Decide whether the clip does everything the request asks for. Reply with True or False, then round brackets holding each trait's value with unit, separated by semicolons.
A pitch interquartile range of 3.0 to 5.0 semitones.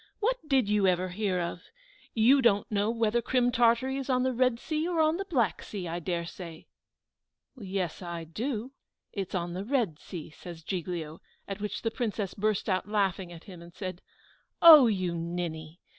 False (5.5 semitones)